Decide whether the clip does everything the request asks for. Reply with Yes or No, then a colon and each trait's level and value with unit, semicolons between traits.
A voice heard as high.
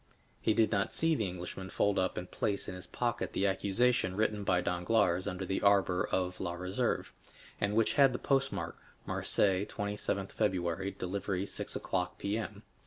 No: low, 100 Hz